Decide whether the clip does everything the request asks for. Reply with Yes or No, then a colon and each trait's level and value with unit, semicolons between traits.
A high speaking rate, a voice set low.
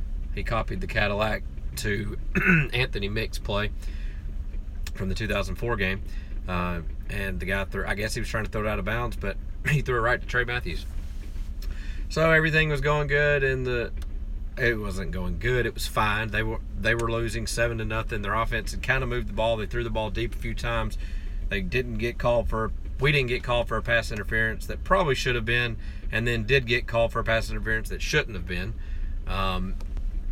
Yes: fast, 215 wpm; low, 110 Hz